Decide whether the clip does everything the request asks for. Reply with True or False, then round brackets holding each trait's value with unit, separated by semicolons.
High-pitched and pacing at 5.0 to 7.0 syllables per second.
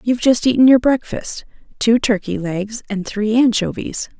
False (225 Hz; 4.8 syllables/s)